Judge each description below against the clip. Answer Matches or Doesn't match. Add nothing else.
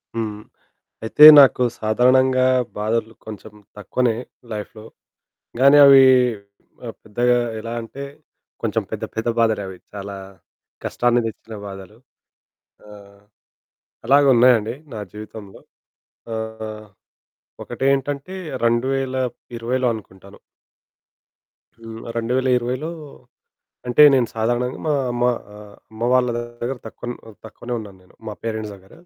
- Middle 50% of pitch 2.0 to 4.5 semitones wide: Matches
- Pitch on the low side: Matches